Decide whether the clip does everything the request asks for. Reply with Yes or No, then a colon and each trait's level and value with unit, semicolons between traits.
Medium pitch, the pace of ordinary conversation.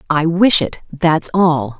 Yes: medium, 165 Hz; average, 165 wpm